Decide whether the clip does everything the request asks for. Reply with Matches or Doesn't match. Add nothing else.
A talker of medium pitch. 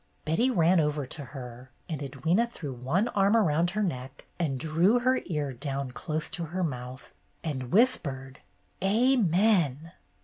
Matches